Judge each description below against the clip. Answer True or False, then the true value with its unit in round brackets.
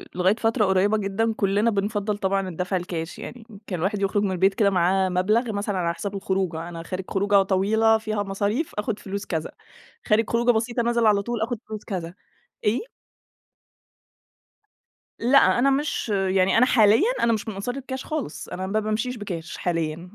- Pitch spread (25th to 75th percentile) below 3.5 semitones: True (3.0 semitones)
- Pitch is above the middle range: True (205 Hz)